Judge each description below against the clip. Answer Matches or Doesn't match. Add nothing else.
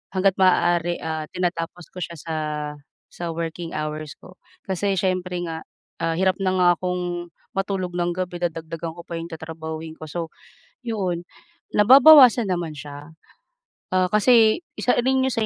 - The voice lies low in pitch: Doesn't match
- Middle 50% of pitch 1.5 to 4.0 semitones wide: Matches